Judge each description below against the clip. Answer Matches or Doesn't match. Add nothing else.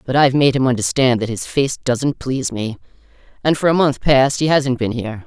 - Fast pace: Matches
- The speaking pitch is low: Matches